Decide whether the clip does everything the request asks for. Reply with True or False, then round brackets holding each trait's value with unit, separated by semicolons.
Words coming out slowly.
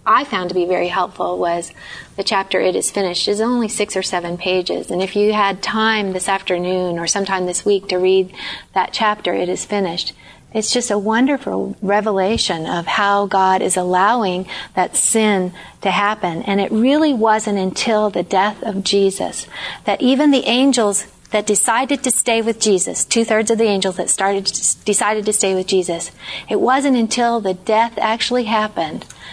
False (180 wpm)